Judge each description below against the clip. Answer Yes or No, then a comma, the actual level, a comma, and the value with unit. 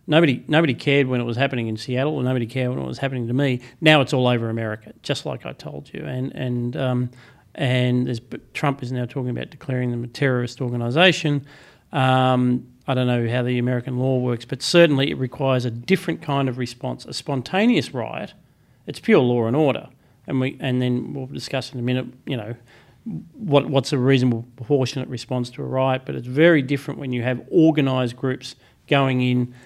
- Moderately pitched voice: No, low, 130 Hz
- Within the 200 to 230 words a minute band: Yes, fast, 205 wpm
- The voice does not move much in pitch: Yes, narrow, 2.2 semitones